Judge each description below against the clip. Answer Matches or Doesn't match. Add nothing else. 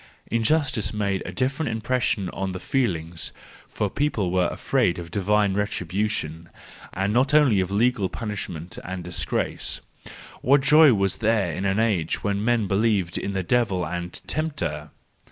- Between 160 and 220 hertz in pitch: Doesn't match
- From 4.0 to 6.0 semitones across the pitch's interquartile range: Matches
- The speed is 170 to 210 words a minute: Doesn't match